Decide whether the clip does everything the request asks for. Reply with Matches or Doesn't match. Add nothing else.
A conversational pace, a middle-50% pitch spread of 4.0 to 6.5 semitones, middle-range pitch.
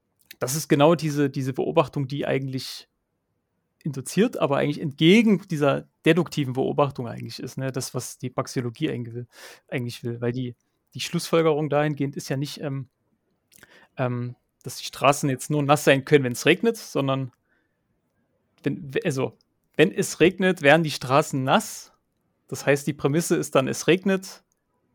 Doesn't match